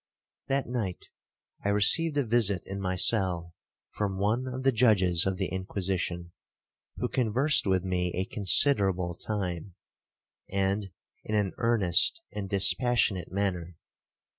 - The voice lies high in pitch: No, low, 100 Hz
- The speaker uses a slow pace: Yes, slow, 130 wpm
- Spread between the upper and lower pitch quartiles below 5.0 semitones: Yes, average, 3.9 semitones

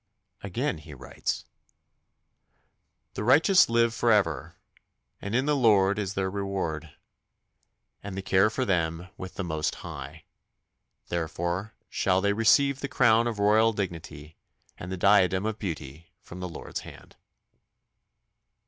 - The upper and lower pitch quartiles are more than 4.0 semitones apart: Yes, average, 4.4 semitones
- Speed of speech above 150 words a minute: No, slow, 135 wpm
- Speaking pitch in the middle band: No, very low, 95 Hz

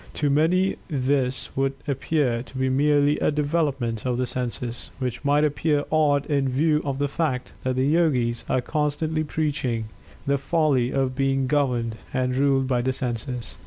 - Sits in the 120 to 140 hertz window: Yes, low, 135 Hz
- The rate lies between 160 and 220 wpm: Yes, average, 165 wpm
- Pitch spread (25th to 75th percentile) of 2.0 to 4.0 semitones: Yes, average, 2.8 semitones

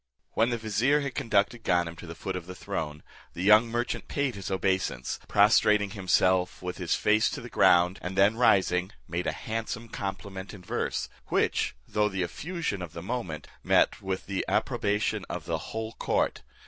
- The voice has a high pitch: No, low, 100 Hz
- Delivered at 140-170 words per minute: No, average, 180 wpm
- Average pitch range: Yes, average, 3.7 semitones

